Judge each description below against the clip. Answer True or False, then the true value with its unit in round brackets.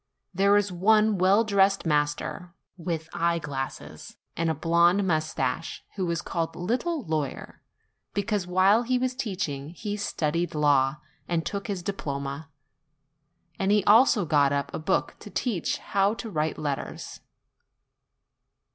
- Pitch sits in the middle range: True (175 Hz)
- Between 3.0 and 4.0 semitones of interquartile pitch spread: False (4.6 semitones)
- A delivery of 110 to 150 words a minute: True (140 wpm)